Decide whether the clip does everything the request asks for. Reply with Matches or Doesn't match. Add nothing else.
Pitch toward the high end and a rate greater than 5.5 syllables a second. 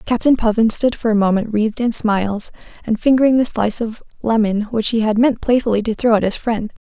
Matches